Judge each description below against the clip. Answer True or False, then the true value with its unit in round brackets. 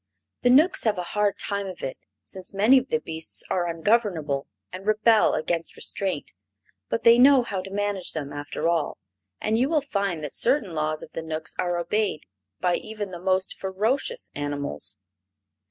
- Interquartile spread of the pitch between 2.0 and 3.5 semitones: False (5.2 semitones)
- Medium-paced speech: True (175 wpm)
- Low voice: False (190 Hz)